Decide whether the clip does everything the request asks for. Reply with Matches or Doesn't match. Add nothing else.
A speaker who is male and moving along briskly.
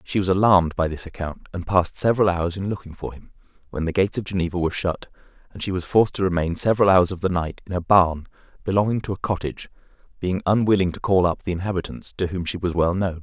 Matches